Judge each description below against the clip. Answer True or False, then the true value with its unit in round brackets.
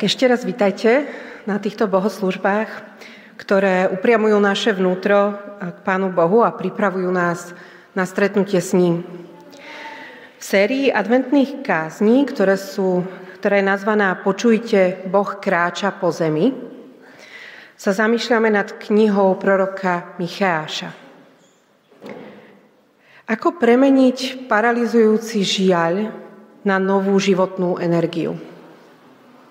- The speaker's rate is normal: False (95 wpm)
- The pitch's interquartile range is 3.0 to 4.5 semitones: True (3.4 semitones)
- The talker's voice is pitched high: True (200 Hz)